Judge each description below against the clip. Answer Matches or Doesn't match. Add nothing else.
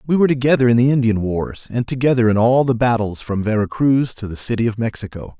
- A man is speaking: Matches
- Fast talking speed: Matches